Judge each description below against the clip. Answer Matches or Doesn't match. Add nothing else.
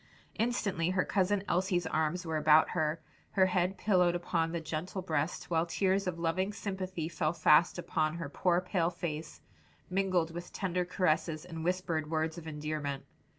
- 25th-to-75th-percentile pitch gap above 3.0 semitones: Doesn't match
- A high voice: Doesn't match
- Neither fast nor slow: Matches